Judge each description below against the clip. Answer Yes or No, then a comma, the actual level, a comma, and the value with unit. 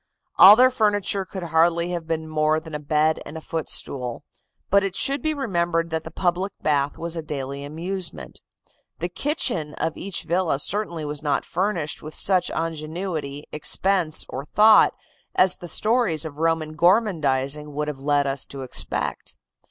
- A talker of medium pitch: Yes, medium, 165 Hz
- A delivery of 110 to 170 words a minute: Yes, average, 165 wpm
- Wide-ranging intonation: No, average, 3.9 semitones